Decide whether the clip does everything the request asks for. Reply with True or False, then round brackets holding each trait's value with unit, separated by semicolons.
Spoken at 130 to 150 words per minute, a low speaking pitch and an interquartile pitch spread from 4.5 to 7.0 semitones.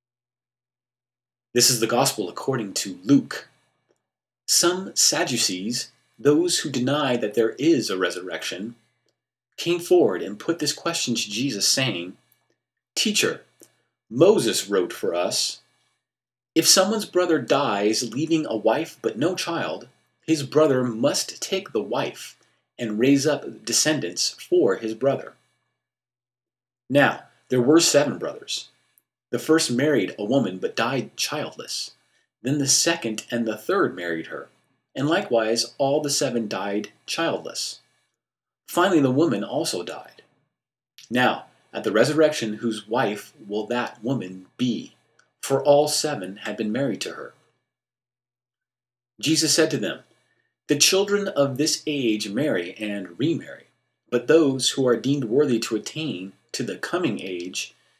True (135 wpm; 125 Hz; 5.2 semitones)